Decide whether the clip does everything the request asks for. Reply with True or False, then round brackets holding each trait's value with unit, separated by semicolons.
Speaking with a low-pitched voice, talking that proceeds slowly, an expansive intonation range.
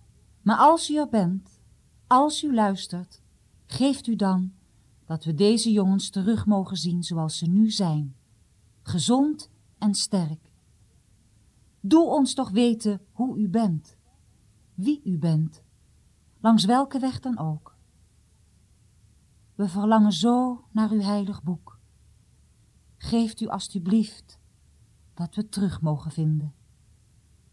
False (195 Hz; 120 wpm; 6.4 semitones)